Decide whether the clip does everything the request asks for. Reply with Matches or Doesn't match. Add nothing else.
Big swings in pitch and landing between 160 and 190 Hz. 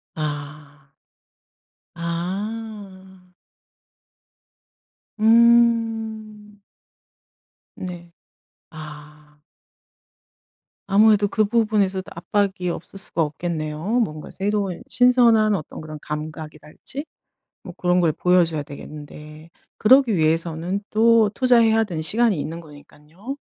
Matches